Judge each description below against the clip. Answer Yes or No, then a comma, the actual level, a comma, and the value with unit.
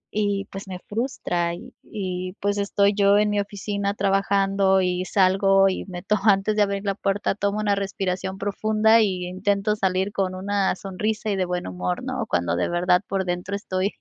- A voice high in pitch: Yes, high, 195 Hz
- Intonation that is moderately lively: No, narrow, 1.6 semitones